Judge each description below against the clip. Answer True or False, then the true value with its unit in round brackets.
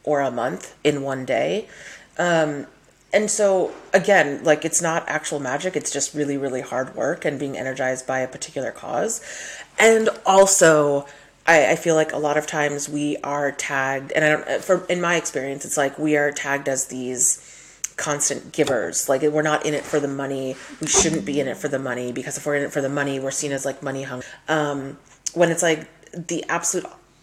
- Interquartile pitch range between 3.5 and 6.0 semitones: False (2.6 semitones)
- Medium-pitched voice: True (145 Hz)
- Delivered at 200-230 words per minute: True (205 wpm)